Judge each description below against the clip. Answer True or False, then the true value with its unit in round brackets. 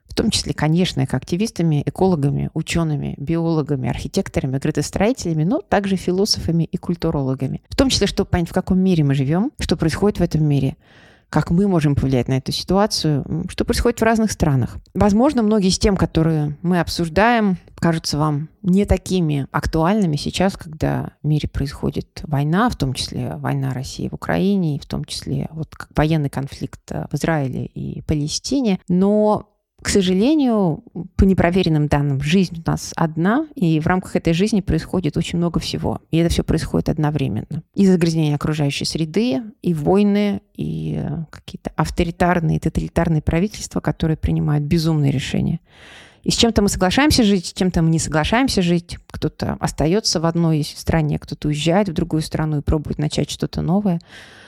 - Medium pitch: True (165 Hz)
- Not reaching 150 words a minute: False (160 wpm)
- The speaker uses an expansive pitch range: False (4.2 semitones)